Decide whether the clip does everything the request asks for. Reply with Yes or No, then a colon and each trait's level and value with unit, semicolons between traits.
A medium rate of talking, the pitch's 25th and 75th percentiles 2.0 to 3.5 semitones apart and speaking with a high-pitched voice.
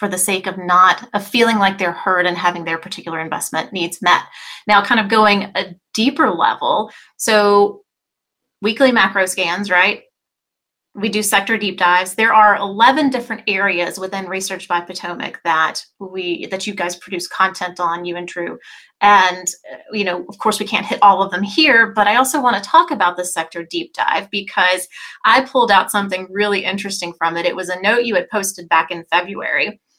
Yes: average, 190 wpm; average, 2.9 semitones; high, 195 Hz